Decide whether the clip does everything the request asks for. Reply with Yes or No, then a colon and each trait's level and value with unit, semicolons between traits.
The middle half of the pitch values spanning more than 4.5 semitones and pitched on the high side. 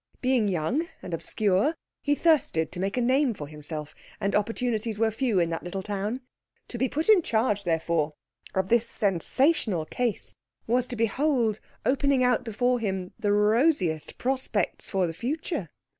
Yes: wide, 5.5 semitones; high, 220 Hz